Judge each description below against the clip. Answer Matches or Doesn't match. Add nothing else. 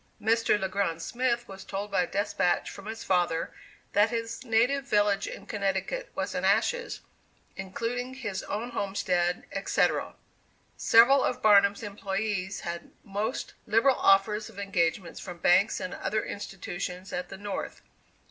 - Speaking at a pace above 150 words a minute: Doesn't match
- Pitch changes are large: Doesn't match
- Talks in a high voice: Matches